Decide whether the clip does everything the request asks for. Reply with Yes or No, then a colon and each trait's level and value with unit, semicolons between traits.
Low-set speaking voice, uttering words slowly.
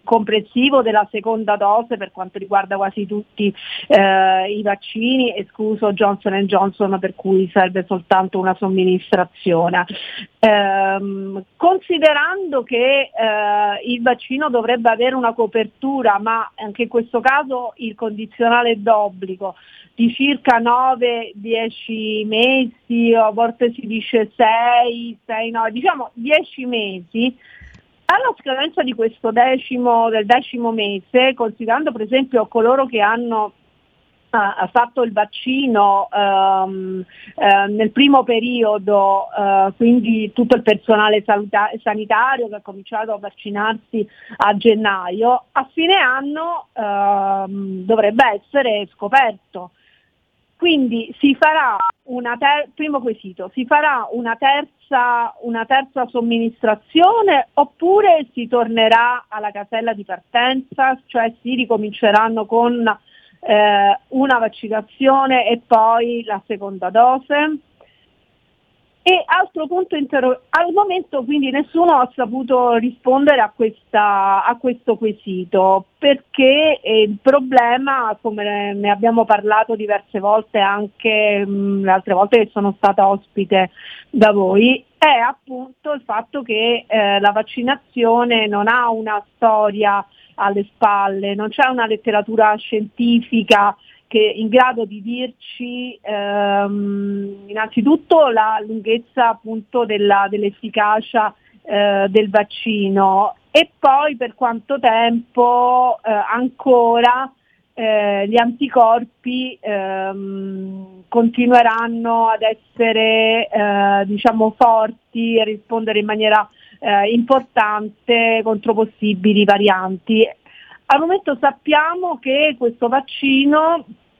No: high, 225 Hz; slow, 110 wpm